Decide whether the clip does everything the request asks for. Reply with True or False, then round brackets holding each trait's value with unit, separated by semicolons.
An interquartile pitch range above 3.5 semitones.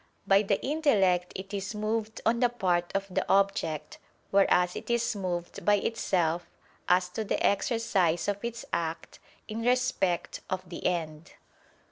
True (4.0 semitones)